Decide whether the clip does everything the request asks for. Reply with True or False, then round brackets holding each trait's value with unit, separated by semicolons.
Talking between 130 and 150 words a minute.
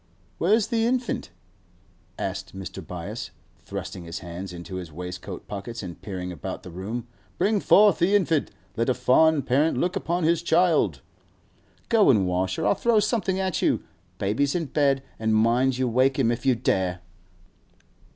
False (165 wpm)